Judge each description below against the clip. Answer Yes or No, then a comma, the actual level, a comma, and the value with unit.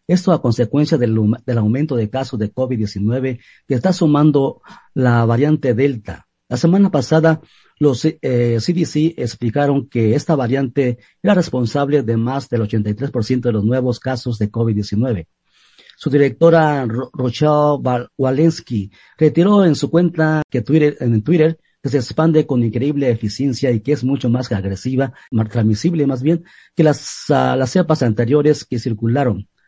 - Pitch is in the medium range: No, low, 130 Hz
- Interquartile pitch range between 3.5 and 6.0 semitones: Yes, average, 4.2 semitones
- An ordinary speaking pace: Yes, average, 150 wpm